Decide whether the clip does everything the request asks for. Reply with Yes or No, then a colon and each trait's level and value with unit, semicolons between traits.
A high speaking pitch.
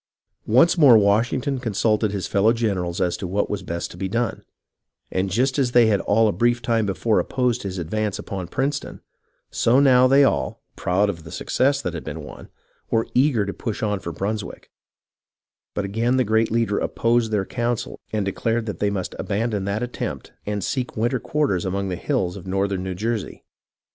No: low, 110 Hz